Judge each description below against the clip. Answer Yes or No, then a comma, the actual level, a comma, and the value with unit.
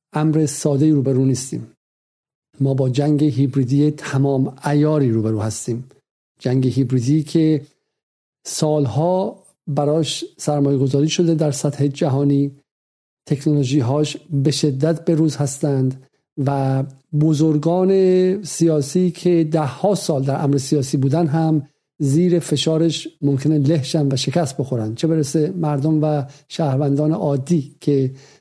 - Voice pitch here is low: No, medium, 150 Hz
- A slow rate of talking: No, average, 125 wpm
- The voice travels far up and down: No, narrow, 2.5 semitones